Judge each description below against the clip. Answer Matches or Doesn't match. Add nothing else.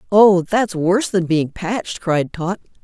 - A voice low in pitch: Doesn't match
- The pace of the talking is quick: Doesn't match